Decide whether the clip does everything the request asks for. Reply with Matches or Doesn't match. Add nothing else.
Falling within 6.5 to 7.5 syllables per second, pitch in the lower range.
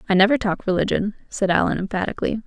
Doesn't match